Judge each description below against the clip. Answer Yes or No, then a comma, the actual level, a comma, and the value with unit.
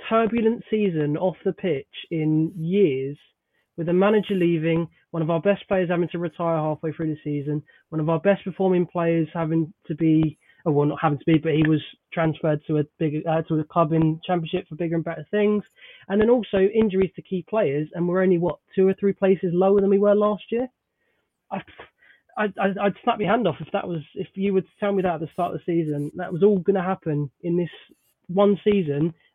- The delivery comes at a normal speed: No, fast, 220 wpm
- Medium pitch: Yes, medium, 175 Hz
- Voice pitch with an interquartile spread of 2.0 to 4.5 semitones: Yes, average, 3.6 semitones